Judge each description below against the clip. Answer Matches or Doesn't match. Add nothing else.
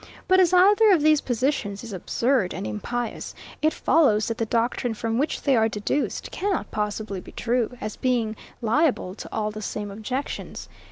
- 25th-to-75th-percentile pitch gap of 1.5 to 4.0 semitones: Doesn't match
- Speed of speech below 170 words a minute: Doesn't match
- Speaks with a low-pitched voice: Doesn't match